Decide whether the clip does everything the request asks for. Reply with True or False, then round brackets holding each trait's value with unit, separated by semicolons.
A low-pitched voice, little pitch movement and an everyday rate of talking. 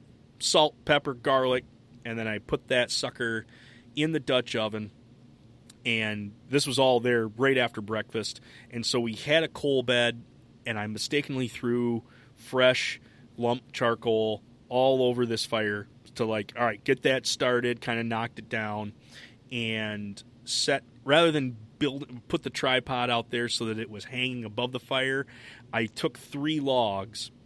True (120 Hz; 2.1 semitones; 160 wpm)